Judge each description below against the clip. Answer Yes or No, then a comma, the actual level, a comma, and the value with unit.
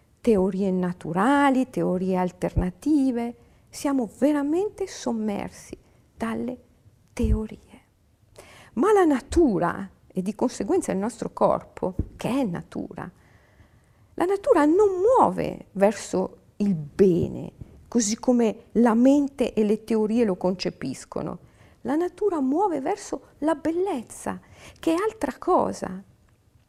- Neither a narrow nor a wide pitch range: No, wide, 8.5 semitones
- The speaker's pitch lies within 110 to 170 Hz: No, high, 240 Hz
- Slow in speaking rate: Yes, slow, 105 wpm